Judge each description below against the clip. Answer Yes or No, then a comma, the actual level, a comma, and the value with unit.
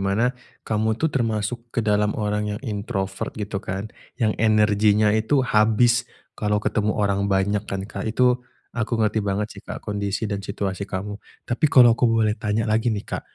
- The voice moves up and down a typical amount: No, narrow, 1.8 semitones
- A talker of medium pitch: No, low, 105 Hz